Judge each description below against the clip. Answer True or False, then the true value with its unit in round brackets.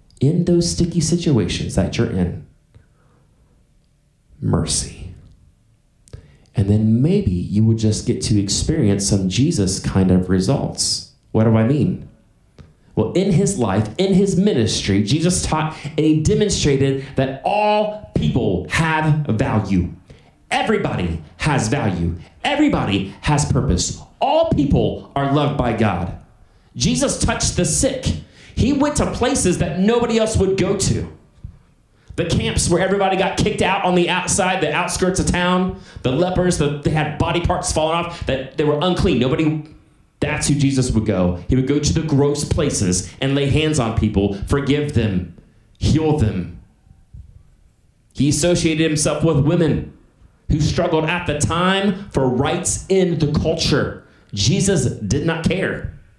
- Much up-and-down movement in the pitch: True (7.9 semitones)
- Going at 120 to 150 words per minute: True (145 wpm)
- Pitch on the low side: False (145 Hz)